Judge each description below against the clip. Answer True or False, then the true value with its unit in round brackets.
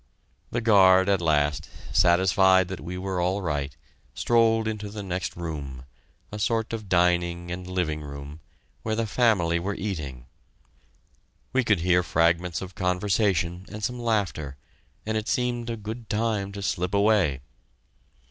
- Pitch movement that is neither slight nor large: True (3.8 semitones)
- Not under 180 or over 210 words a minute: False (150 wpm)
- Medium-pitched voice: False (95 Hz)